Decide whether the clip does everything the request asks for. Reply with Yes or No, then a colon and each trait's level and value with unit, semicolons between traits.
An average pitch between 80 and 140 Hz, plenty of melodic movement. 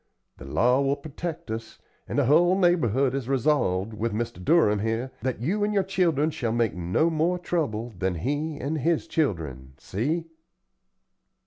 Yes: low, 135 Hz; wide, 6.5 semitones